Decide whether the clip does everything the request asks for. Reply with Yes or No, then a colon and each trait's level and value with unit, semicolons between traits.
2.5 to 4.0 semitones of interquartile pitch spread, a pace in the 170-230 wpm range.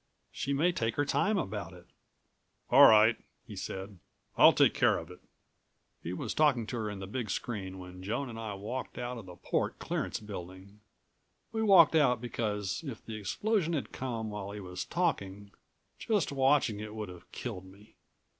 No: wide, 5.5 semitones; average, 185 wpm